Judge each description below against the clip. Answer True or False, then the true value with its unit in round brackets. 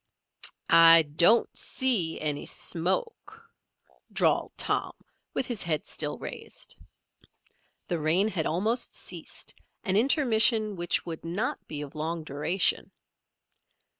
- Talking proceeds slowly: True (110 wpm)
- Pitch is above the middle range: False (175 Hz)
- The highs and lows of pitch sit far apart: True (5.7 semitones)